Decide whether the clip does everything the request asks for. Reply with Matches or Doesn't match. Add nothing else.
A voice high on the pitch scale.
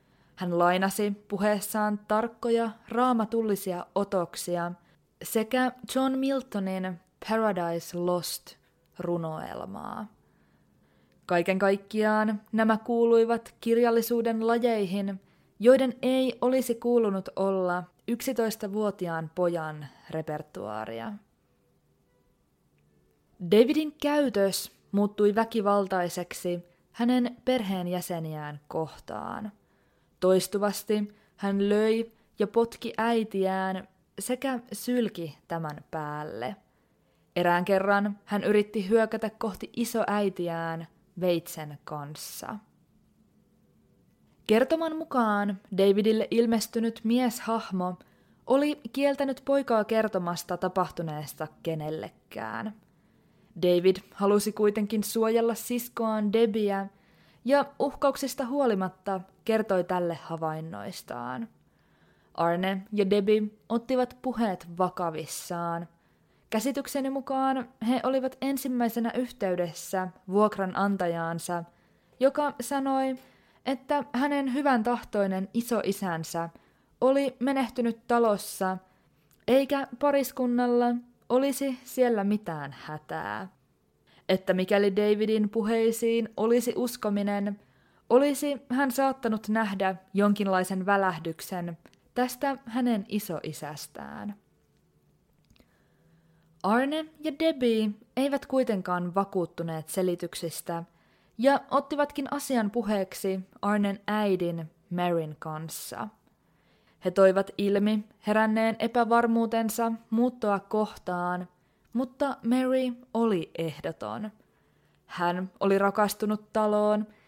Matches